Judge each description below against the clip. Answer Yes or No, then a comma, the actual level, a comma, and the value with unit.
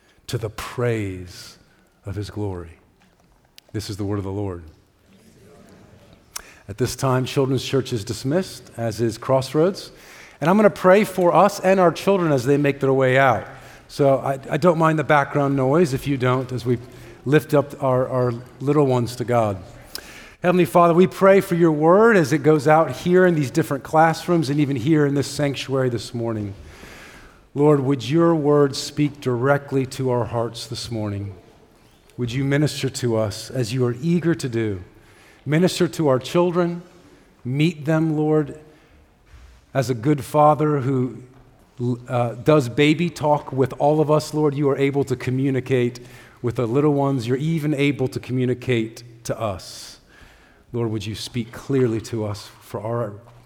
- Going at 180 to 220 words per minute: No, average, 170 wpm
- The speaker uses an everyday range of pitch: Yes, average, 4.3 semitones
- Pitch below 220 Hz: Yes, low, 135 Hz